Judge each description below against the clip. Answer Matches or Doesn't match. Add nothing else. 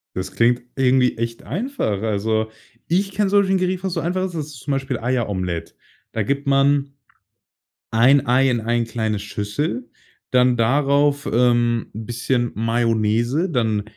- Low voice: Matches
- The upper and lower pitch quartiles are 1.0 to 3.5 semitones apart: Doesn't match